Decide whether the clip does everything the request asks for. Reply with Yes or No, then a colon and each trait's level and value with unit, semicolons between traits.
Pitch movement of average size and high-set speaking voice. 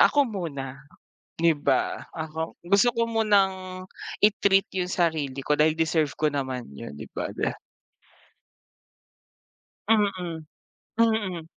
No: average, 4.7 semitones; medium, 175 Hz